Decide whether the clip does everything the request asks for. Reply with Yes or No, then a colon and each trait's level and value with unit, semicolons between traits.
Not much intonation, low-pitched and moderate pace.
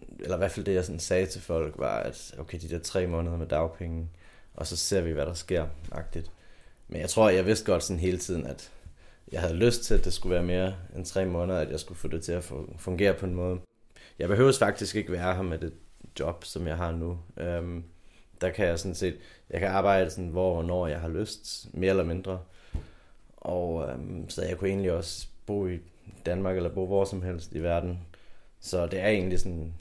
No: narrow, 2.1 semitones; very low, 90 Hz; fast, 230 wpm